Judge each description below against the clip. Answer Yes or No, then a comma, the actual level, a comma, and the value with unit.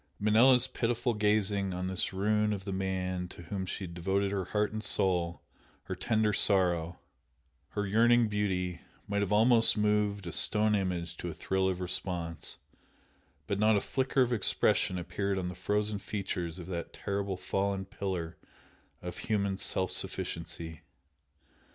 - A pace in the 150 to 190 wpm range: Yes, average, 155 wpm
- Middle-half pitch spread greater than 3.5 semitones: No, narrow, 2.5 semitones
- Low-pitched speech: Yes, low, 100 Hz